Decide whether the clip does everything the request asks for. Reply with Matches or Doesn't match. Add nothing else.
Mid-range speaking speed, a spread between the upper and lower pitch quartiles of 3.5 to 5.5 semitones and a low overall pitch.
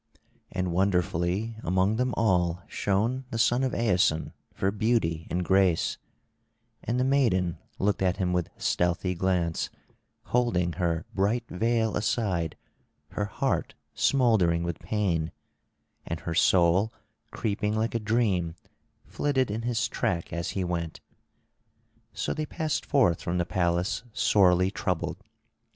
Doesn't match